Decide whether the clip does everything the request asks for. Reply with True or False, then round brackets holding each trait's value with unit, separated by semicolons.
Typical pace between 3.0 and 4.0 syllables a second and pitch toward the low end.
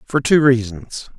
True (3.9 syllables/s; 125 Hz)